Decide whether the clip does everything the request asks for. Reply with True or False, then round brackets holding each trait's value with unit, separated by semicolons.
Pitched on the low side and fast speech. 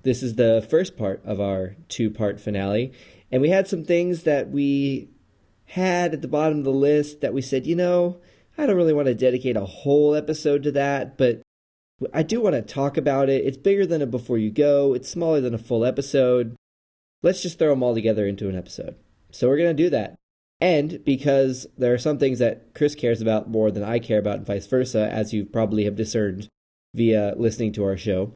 True (125 Hz; 220 wpm)